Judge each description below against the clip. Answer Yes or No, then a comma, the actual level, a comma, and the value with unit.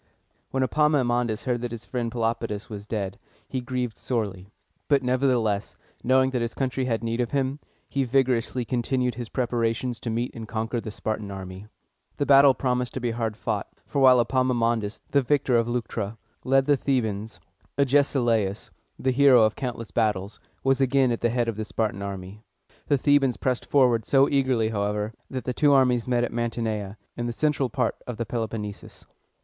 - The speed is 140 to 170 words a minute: No, average, 180 wpm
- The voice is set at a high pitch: No, low, 120 Hz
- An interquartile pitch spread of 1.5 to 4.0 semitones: Yes, average, 2.9 semitones